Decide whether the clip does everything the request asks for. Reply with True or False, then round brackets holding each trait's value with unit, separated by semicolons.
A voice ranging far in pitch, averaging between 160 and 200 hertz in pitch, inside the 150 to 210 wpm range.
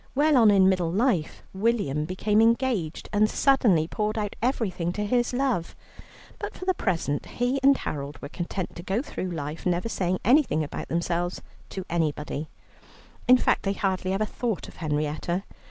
True (5.7 semitones; 190 Hz; 170 wpm)